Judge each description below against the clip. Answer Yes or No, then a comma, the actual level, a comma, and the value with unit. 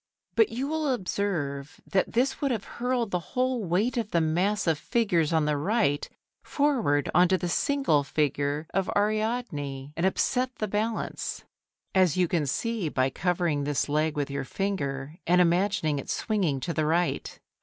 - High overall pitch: No, medium, 180 Hz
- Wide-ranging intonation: Yes, wide, 6.8 semitones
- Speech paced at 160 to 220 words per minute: Yes, average, 170 wpm